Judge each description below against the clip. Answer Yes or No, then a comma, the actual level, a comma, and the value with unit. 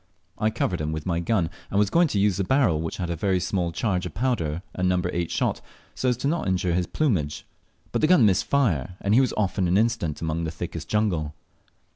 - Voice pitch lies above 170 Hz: No, very low, 90 Hz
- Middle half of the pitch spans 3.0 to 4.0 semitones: No, average, 4.6 semitones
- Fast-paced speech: Yes, fast, 240 wpm